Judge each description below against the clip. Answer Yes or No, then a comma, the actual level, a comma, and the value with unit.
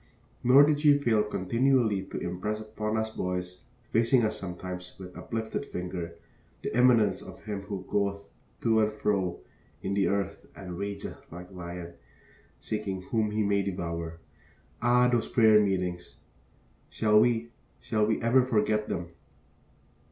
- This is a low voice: Yes, low, 105 Hz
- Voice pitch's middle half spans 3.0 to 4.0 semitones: Yes, average, 3.6 semitones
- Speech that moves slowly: No, average, 145 wpm